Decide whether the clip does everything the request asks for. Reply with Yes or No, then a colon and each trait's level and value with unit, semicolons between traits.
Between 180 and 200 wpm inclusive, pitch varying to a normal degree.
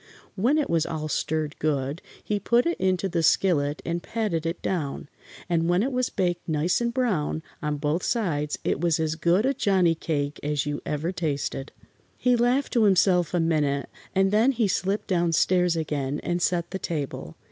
Yes: average, 190 wpm; average, 4.3 semitones